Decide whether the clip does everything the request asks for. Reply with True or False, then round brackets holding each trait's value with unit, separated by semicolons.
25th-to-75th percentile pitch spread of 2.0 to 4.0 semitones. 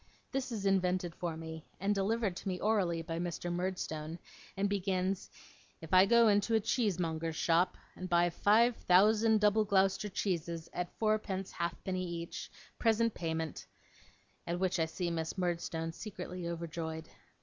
True (3.3 semitones)